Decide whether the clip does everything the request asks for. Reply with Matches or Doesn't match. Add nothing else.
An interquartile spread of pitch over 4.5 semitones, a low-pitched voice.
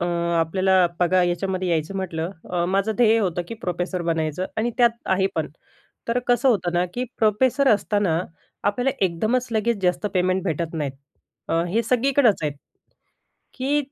Doesn't match